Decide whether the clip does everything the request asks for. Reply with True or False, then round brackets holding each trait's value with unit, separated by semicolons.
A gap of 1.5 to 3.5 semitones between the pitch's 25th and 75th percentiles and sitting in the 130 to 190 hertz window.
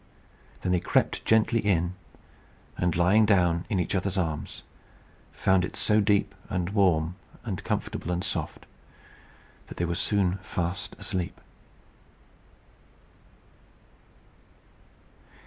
False (2.5 semitones; 90 Hz)